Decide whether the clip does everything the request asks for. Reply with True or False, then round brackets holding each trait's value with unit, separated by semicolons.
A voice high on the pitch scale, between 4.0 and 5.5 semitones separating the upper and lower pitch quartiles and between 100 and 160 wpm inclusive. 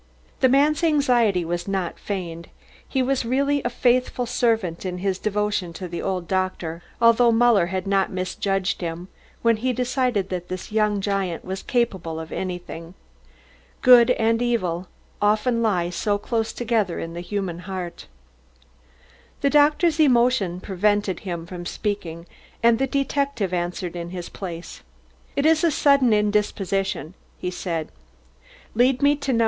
True (205 Hz; 5.2 semitones; 150 wpm)